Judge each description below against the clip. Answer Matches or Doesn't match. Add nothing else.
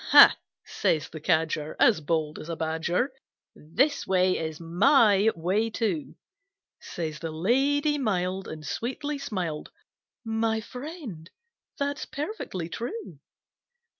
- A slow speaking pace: Matches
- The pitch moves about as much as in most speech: Doesn't match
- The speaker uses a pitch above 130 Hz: Matches